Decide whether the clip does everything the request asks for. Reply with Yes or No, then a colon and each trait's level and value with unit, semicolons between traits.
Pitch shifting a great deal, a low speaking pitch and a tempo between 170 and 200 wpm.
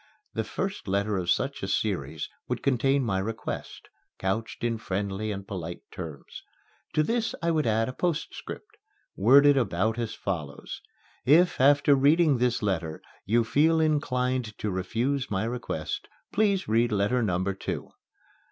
No: wide, 6.3 semitones; low, 115 Hz; average, 145 wpm